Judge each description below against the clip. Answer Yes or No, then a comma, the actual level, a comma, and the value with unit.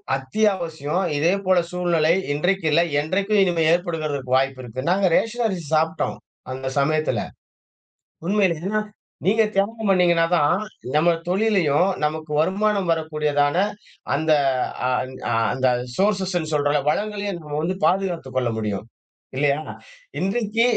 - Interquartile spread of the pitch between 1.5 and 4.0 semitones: No, average, 4.7 semitones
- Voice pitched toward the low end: No, medium, 165 Hz